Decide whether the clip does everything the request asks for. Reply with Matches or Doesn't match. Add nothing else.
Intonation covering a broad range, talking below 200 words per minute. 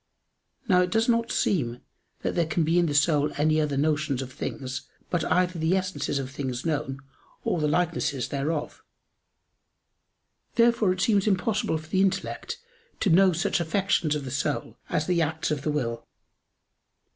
Doesn't match